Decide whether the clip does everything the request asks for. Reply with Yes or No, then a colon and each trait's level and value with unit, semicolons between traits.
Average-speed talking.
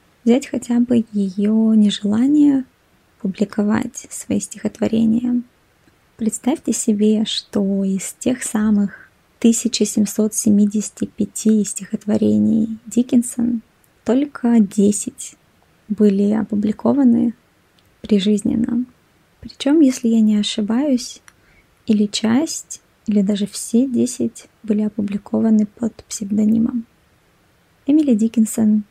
No: slow, 80 wpm